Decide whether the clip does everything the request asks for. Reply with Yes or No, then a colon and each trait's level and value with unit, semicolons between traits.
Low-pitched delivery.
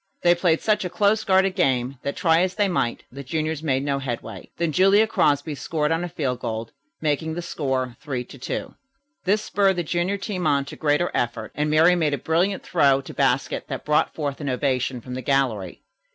No: medium, 150 Hz